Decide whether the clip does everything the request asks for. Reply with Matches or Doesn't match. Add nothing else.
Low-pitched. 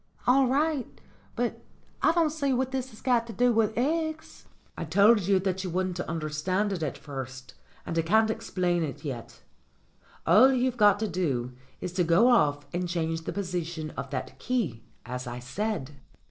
Doesn't match